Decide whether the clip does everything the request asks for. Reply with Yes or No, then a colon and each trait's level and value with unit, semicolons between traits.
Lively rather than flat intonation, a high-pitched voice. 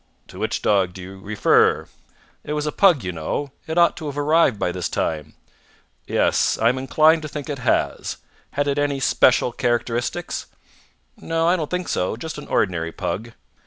No: wide, 7.3 semitones; low, 135 Hz